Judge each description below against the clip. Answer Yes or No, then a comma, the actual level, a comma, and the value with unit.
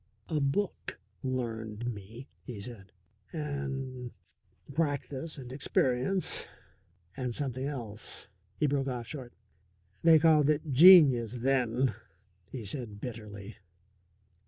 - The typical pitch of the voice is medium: No, low, 130 Hz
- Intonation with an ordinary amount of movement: Yes, average, 3.6 semitones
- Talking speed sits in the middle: No, slow, 105 wpm